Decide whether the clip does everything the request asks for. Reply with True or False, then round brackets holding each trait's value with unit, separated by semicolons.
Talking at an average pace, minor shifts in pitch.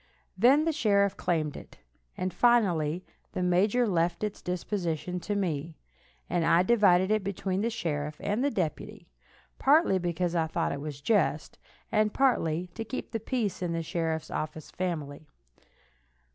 False (150 wpm; 4.6 semitones)